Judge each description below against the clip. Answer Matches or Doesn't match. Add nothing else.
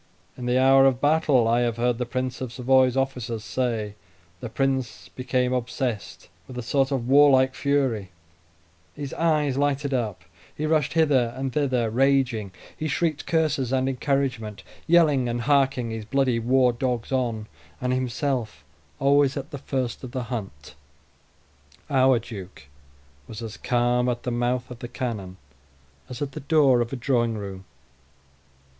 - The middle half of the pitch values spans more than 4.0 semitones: Doesn't match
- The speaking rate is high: Doesn't match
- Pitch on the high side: Doesn't match